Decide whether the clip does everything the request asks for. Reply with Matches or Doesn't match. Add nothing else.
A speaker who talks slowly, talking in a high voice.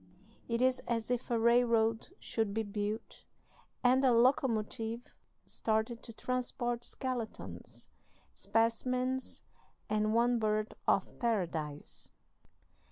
Matches